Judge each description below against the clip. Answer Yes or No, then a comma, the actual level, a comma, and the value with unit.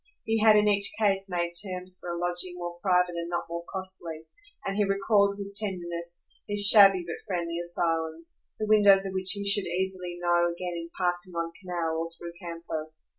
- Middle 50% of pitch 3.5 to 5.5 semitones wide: No, narrow, 2.5 semitones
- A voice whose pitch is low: No, medium, 180 Hz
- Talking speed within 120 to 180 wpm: No, average, 190 wpm